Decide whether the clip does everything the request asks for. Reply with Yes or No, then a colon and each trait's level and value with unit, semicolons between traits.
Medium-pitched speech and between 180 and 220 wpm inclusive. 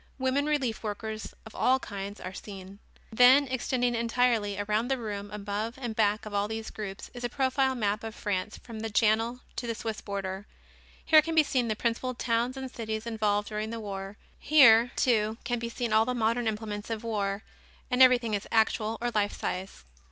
No: high, 225 Hz; average, 195 wpm